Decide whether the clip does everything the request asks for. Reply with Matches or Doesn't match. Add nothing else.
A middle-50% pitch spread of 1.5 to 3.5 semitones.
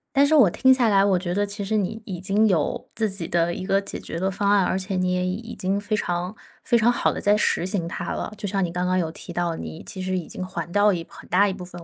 Matches